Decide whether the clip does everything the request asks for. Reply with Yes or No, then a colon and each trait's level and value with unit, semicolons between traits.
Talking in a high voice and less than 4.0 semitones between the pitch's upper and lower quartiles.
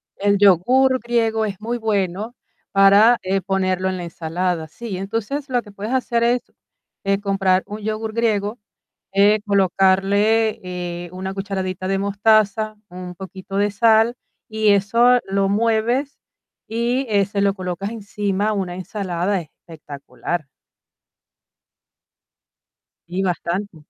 Yes: high, 200 Hz; average, 2.8 semitones